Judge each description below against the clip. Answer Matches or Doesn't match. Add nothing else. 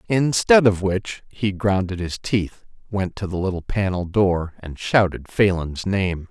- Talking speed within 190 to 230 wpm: Doesn't match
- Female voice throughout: Doesn't match